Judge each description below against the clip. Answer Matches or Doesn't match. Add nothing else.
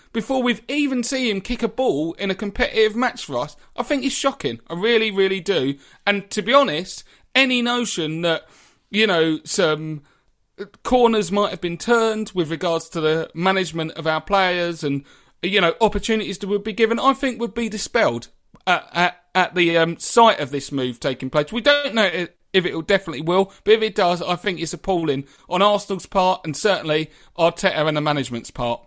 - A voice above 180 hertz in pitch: Matches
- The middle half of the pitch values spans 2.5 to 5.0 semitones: Doesn't match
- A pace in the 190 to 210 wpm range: Matches